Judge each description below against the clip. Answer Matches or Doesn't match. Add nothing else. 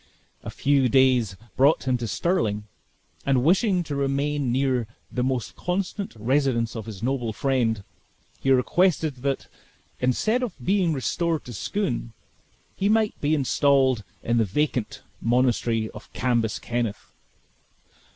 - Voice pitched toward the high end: Doesn't match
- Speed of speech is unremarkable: Doesn't match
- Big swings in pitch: Doesn't match